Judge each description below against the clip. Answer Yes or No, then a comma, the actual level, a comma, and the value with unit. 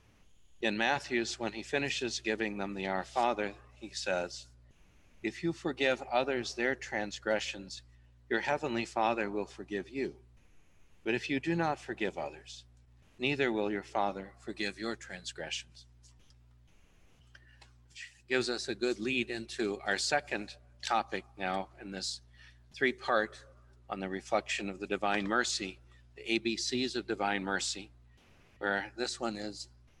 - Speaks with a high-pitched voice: No, low, 100 Hz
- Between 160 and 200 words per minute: No, average, 140 wpm